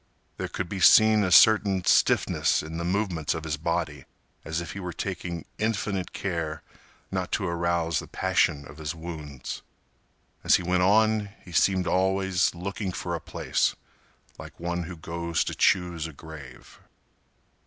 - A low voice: Yes, very low, 85 Hz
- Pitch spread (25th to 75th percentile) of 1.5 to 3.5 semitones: Yes, average, 2.8 semitones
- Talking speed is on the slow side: No, average, 160 wpm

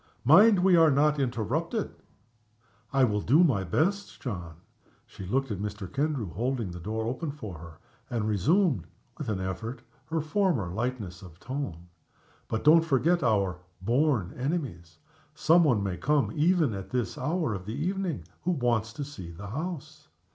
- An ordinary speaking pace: Yes, average, 160 wpm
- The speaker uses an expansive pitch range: Yes, wide, 7.7 semitones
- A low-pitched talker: Yes, low, 125 Hz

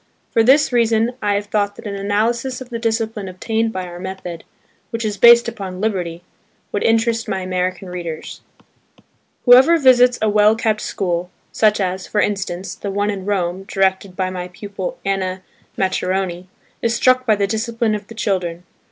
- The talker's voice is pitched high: Yes, high, 205 Hz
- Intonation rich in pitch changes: No, average, 3.4 semitones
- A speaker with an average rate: Yes, average, 165 wpm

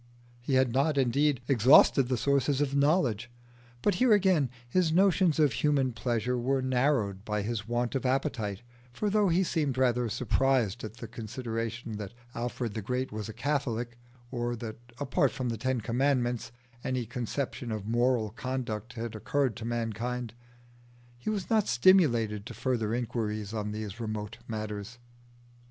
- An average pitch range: Yes, average, 3.4 semitones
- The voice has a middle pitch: No, low, 120 Hz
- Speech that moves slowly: No, average, 155 wpm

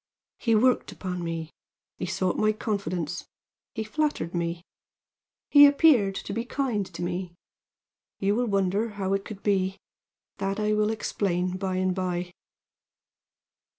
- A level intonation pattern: No, average, 3.0 semitones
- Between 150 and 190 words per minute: No, average, 140 wpm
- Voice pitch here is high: Yes, high, 195 Hz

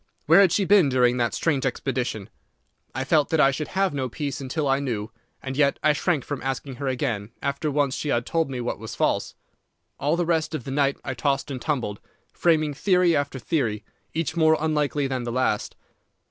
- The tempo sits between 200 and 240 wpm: Yes, fast, 205 wpm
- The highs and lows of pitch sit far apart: No, average, 3.4 semitones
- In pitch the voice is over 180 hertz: No, medium, 140 Hz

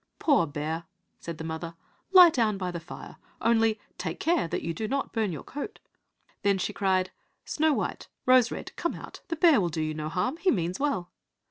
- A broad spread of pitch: Yes, wide, 8.6 semitones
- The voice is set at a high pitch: Yes, high, 195 Hz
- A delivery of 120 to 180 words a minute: No, fast, 205 wpm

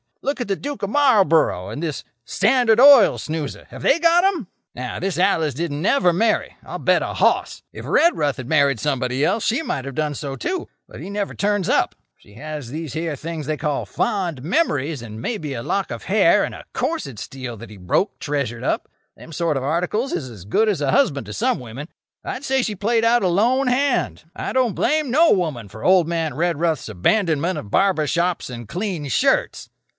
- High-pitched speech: No, medium, 165 Hz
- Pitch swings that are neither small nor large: No, wide, 8.0 semitones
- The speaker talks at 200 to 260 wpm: Yes, fast, 205 wpm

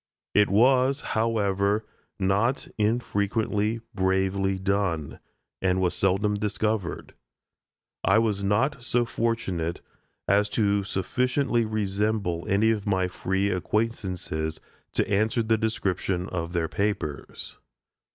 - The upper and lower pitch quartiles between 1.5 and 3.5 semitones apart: Yes, average, 2.8 semitones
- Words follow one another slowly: Yes, slow, 105 wpm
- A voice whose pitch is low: Yes, low, 100 Hz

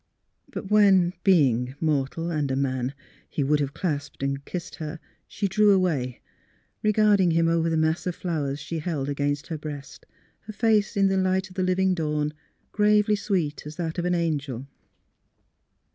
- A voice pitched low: No, medium, 165 Hz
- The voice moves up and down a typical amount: Yes, average, 4.7 semitones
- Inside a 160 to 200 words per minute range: Yes, average, 170 wpm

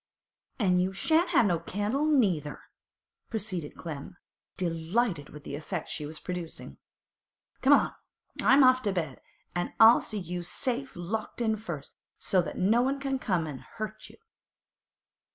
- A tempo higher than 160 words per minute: No, average, 150 wpm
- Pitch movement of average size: No, wide, 6.0 semitones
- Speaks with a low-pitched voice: No, high, 190 Hz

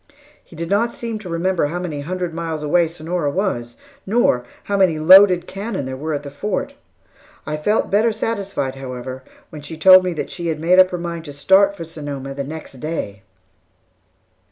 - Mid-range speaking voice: Yes, medium, 165 Hz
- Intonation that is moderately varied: Yes, average, 4.4 semitones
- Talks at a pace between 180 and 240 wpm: Yes, average, 190 wpm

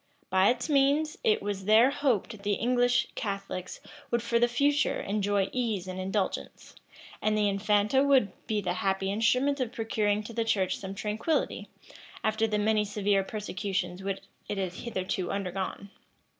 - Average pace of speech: Yes, average, 155 wpm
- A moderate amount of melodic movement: Yes, average, 3.3 semitones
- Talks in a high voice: Yes, high, 210 Hz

